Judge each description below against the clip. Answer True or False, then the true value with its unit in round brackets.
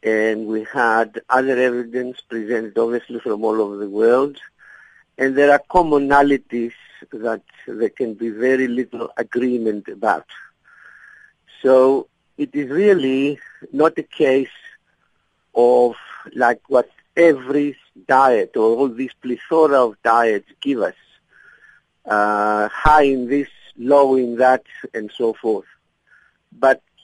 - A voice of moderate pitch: False (125 Hz)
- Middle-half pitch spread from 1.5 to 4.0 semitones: True (3.5 semitones)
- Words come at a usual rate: False (120 wpm)